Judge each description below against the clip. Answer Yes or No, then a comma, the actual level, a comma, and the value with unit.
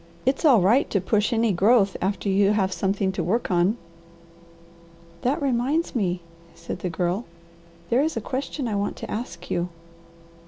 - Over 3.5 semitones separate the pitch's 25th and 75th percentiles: Yes, average, 4.6 semitones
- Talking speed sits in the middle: Yes, average, 165 wpm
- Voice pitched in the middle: No, high, 205 Hz